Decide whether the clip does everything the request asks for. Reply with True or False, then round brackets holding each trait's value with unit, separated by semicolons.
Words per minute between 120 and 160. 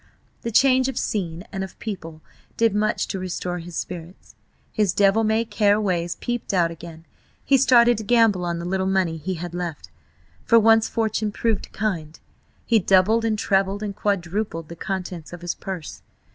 False (175 wpm)